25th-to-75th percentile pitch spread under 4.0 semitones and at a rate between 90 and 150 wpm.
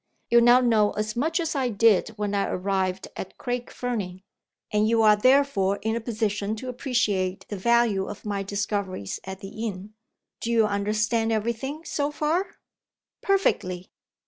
No: average, 3.2 semitones; average, 165 wpm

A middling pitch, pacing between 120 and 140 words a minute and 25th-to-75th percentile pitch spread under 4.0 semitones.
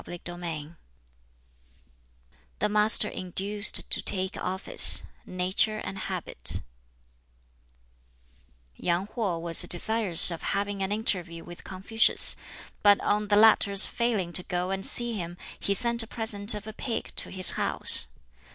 No: high, 195 Hz; slow, 135 wpm; average, 3.0 semitones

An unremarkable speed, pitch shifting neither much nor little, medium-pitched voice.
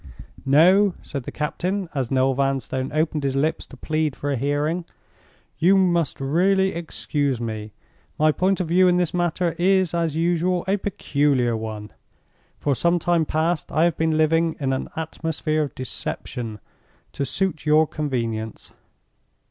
Yes: average, 155 wpm; average, 4.2 semitones; medium, 155 Hz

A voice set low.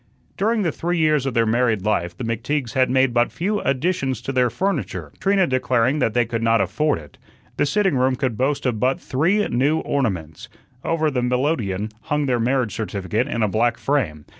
Yes: low, 130 Hz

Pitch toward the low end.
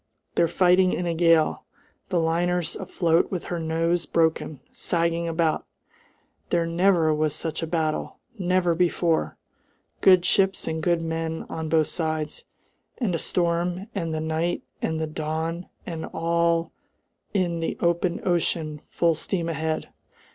No: medium, 165 Hz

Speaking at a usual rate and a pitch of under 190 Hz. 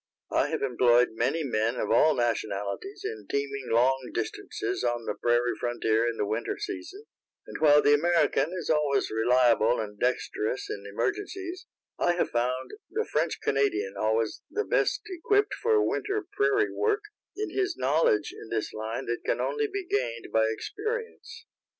Yes: average, 160 wpm; low, 135 Hz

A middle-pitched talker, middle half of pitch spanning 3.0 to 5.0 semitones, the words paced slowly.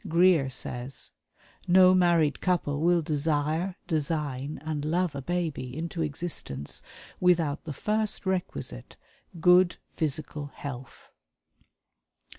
Yes: medium, 160 Hz; average, 3.7 semitones; slow, 100 wpm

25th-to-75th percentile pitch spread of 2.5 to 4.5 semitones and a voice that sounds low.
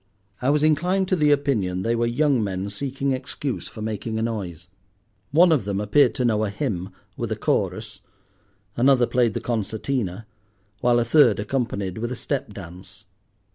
No: average, 5.3 semitones; low, 115 Hz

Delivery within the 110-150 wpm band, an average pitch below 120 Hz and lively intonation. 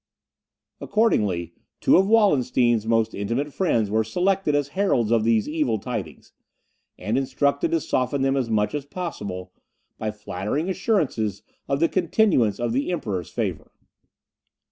No: average, 140 wpm; low, 125 Hz; wide, 7.5 semitones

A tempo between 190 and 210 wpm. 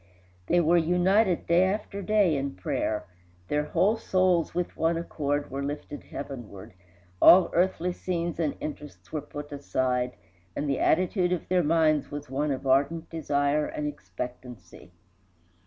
No: average, 145 wpm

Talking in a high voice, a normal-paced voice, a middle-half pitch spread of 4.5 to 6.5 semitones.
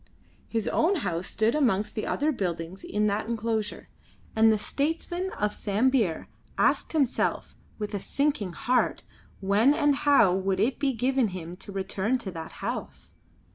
Yes: high, 220 Hz; average, 155 wpm; wide, 5.6 semitones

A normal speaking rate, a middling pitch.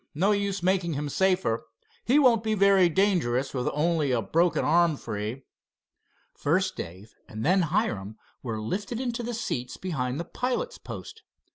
Yes: average, 155 wpm; medium, 170 Hz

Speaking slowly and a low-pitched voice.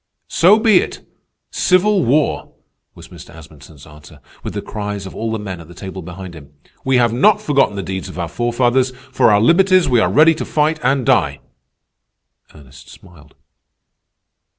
No: average, 175 wpm; low, 110 Hz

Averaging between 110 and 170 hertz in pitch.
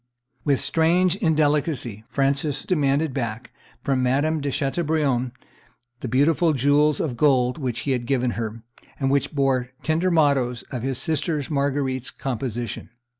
Yes: medium, 140 Hz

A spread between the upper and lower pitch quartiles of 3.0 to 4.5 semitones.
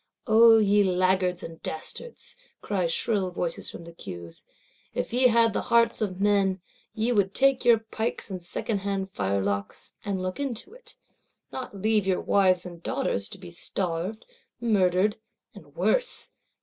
Yes: average, 3.8 semitones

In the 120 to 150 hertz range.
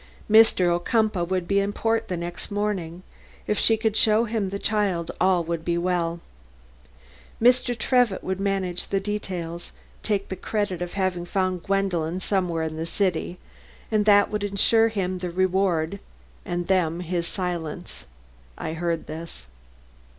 No: medium, 185 Hz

